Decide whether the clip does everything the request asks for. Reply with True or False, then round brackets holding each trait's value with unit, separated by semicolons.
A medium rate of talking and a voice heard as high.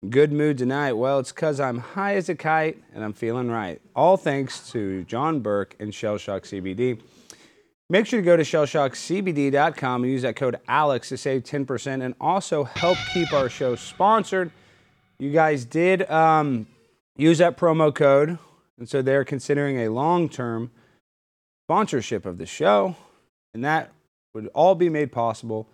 False (165 wpm; 140 Hz)